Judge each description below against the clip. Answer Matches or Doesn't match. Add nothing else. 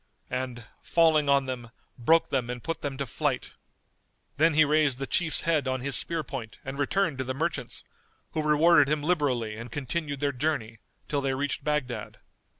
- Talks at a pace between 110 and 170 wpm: Doesn't match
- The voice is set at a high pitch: Doesn't match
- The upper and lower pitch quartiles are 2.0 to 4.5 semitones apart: Matches